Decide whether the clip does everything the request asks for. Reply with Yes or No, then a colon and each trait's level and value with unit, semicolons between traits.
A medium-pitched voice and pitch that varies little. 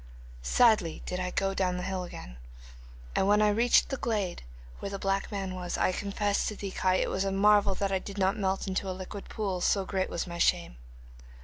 No: high, 195 Hz; narrow, 1.7 semitones